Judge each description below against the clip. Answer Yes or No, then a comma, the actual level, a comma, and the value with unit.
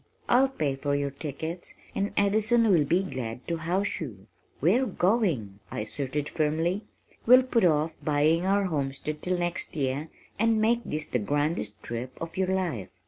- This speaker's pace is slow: No, average, 165 wpm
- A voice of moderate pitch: Yes, medium, 160 Hz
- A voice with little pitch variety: No, wide, 5.6 semitones